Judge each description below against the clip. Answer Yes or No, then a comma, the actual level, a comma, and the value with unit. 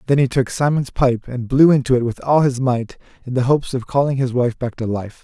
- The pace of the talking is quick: Yes, fast, 265 wpm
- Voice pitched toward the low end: Yes, low, 130 Hz